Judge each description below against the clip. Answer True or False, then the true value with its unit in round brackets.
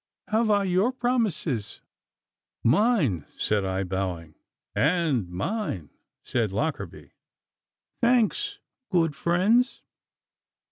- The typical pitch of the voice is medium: True (170 Hz)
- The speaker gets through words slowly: True (85 wpm)